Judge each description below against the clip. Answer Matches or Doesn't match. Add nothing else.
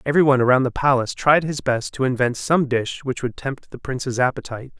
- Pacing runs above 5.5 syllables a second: Matches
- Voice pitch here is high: Doesn't match